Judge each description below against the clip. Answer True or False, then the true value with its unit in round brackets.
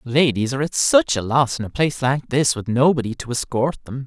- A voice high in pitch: False (130 Hz)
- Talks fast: True (235 wpm)